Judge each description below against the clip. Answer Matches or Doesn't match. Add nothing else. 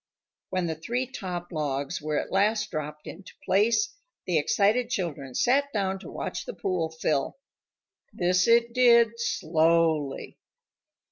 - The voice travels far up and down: Matches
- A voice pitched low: Doesn't match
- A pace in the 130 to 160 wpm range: Matches